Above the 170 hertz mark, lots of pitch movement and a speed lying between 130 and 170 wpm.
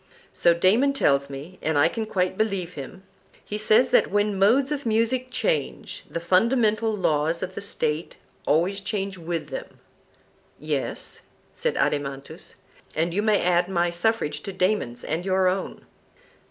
No: high, 190 Hz; average, 4.3 semitones; average, 150 wpm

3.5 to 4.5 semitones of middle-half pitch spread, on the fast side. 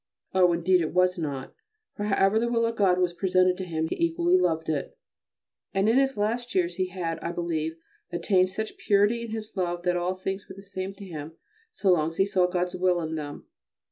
No: narrow, 2.5 semitones; fast, 220 wpm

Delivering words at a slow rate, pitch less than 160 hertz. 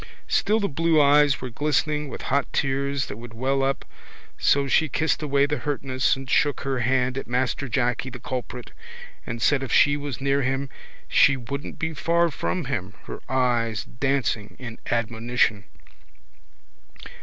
No: average, 160 wpm; low, 135 Hz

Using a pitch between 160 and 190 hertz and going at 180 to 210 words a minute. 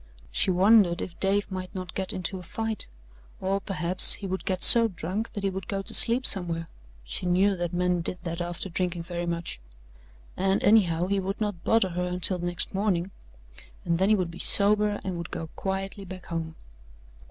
Yes: medium, 185 Hz; average, 195 wpm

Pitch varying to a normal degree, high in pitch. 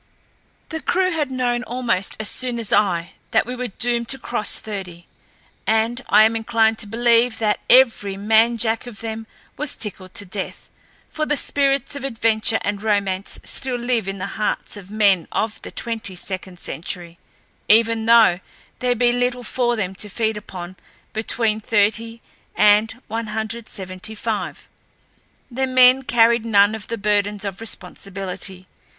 Yes: average, 3.0 semitones; high, 220 Hz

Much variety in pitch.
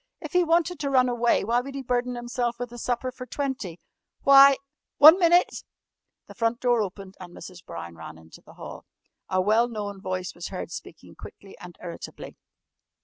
Yes: wide, 5.8 semitones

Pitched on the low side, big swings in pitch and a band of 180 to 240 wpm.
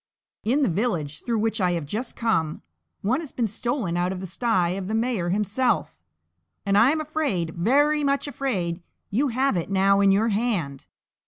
No: high, 210 Hz; wide, 5.7 semitones; average, 185 wpm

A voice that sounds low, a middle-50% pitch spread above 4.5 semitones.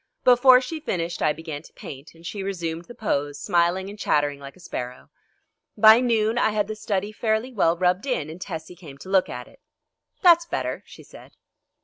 No: medium, 185 Hz; average, 5.2 semitones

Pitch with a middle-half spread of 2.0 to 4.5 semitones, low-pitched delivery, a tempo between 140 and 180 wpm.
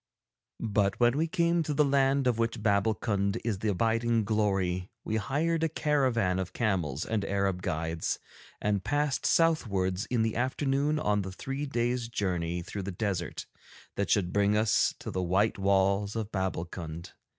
No: average, 4.9 semitones; low, 105 Hz; average, 160 wpm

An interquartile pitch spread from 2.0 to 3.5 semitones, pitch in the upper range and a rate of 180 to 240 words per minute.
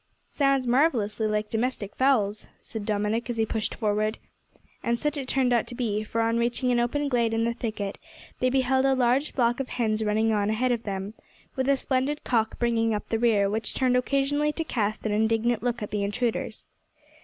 Yes: average, 3.0 semitones; high, 235 Hz; average, 200 wpm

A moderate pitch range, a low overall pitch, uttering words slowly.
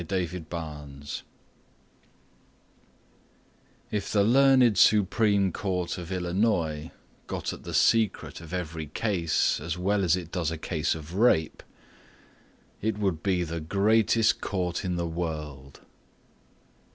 Yes: average, 3.9 semitones; very low, 90 Hz; slow, 120 wpm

